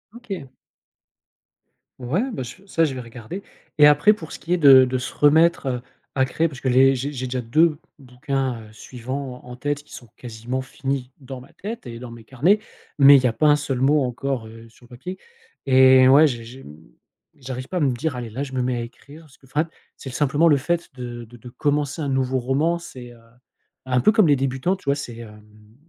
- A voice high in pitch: No, low, 130 Hz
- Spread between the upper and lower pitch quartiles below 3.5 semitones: Yes, average, 3.1 semitones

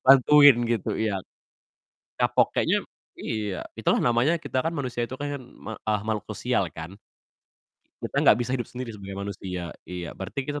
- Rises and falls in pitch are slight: No, average, 5.0 semitones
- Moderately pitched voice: No, low, 120 Hz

